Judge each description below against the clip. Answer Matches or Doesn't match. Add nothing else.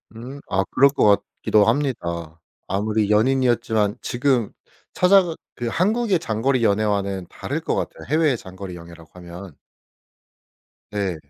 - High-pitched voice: Doesn't match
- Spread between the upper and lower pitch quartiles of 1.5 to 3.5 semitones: Doesn't match